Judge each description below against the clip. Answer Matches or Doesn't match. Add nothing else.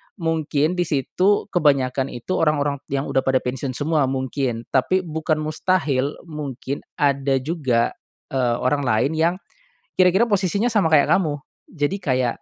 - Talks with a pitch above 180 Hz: Doesn't match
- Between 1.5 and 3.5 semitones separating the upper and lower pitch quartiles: Doesn't match